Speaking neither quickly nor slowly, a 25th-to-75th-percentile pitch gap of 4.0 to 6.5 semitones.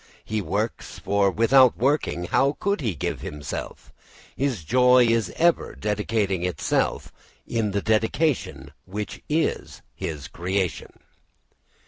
No: slow, 115 wpm; average, 5.1 semitones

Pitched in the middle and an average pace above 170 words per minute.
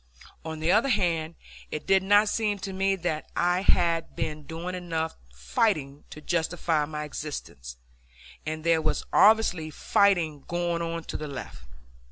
No: medium, 165 Hz; average, 155 wpm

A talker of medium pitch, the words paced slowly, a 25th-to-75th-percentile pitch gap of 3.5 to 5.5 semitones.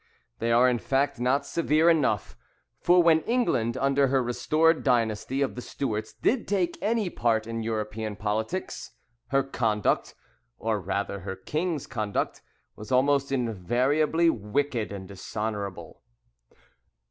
No: low, 125 Hz; slow, 130 wpm; average, 5.2 semitones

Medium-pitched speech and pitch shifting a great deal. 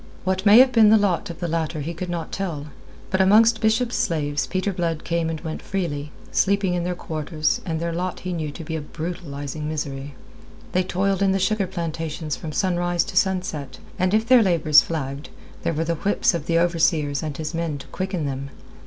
No: medium, 170 Hz; average, 3.5 semitones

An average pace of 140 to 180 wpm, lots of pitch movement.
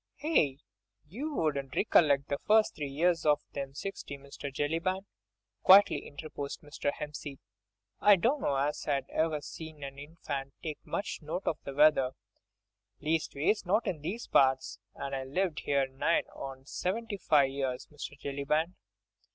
No: average, 145 wpm; average, 3.8 semitones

